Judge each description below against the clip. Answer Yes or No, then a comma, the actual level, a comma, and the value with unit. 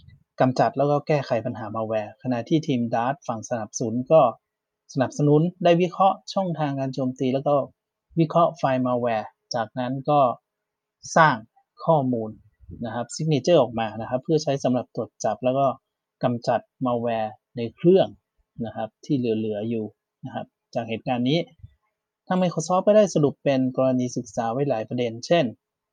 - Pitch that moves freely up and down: No, average, 4.7 semitones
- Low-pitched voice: Yes, low, 130 Hz